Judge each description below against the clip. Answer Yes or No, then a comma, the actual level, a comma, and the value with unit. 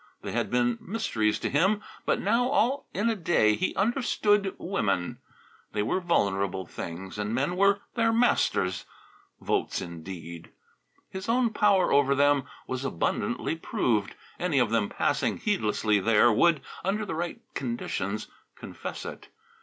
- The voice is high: No, medium, 145 Hz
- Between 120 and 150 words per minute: Yes, average, 145 wpm